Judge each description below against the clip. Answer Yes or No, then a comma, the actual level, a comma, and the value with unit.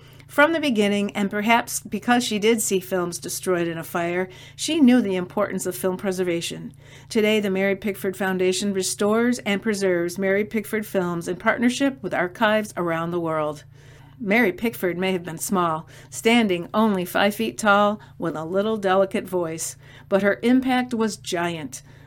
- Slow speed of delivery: No, average, 165 wpm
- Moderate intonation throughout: Yes, average, 3.9 semitones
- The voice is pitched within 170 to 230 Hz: Yes, high, 190 Hz